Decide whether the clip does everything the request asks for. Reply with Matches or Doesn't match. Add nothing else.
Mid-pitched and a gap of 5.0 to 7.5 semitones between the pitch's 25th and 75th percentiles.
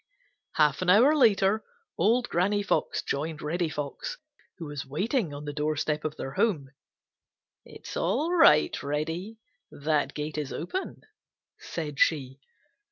Matches